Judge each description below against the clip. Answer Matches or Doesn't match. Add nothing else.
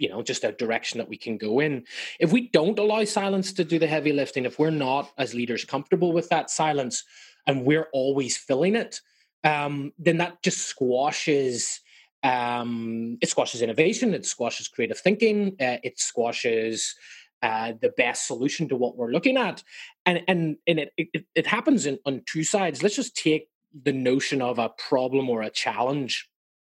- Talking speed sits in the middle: Matches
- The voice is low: Doesn't match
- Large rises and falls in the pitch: Matches